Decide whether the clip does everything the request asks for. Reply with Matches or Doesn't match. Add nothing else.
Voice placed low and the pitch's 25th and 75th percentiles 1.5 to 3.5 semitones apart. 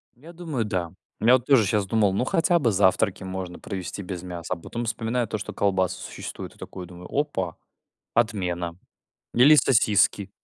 Doesn't match